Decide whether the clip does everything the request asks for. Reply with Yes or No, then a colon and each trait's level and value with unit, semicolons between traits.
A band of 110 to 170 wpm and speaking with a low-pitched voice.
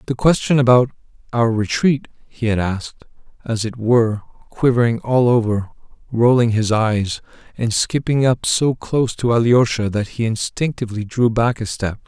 Yes: average, 155 wpm; low, 115 Hz